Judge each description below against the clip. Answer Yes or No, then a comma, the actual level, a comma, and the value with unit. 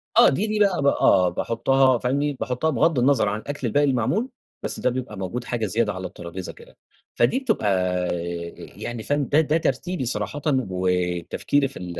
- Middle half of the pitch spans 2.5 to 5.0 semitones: No, wide, 5.6 semitones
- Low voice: Yes, low, 125 Hz